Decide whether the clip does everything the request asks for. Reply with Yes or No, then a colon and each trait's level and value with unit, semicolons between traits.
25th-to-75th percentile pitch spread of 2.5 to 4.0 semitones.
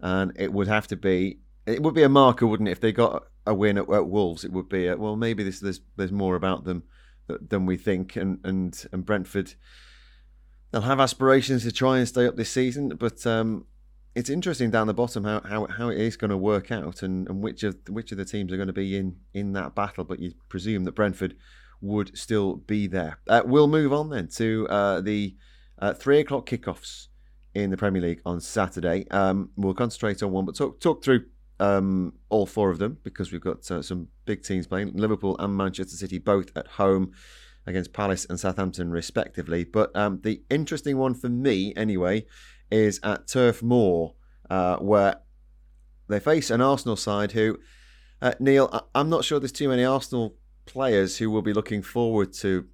Yes: average, 3.6 semitones